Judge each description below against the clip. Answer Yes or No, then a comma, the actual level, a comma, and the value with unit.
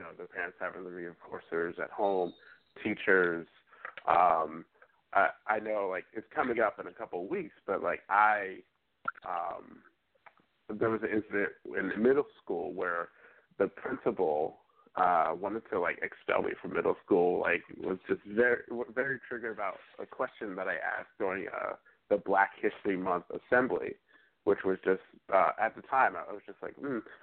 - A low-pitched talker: Yes, low, 110 Hz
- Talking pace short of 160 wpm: No, average, 170 wpm